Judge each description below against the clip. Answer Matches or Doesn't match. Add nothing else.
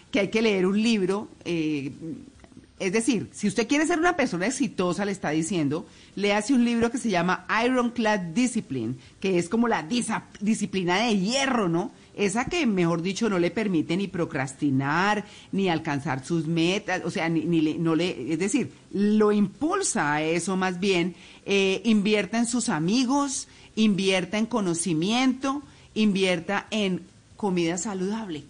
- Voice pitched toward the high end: Matches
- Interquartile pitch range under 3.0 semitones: Doesn't match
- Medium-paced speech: Matches